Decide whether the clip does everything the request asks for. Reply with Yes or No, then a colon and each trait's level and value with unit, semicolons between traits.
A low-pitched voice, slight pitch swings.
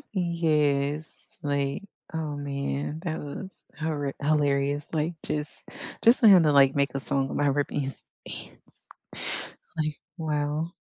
No: medium, 145 Hz; narrow, 2.0 semitones